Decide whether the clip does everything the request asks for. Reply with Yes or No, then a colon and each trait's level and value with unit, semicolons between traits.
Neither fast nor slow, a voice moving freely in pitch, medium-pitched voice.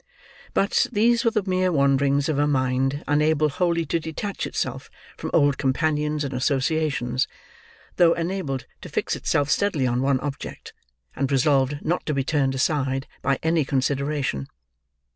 No: average, 150 wpm; average, 3.1 semitones; medium, 145 Hz